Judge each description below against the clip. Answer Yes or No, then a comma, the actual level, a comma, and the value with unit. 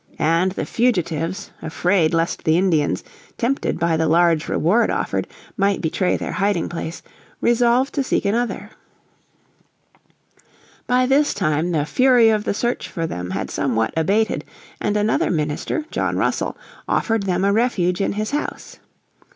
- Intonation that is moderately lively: No, wide, 5.8 semitones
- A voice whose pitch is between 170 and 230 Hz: Yes, medium, 185 Hz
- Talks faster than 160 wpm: No, average, 145 wpm